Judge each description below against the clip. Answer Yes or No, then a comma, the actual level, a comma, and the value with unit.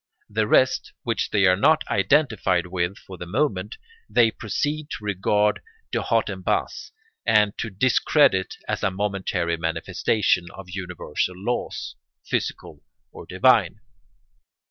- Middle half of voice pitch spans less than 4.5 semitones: Yes, average, 3.4 semitones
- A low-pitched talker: Yes, low, 100 Hz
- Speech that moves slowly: Yes, slow, 130 wpm